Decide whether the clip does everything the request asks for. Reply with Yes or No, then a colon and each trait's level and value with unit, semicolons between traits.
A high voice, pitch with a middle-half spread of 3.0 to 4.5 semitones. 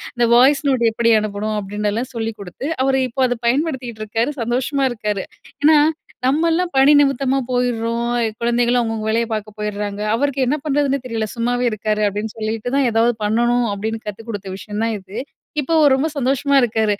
Yes: high, 235 Hz; average, 3.7 semitones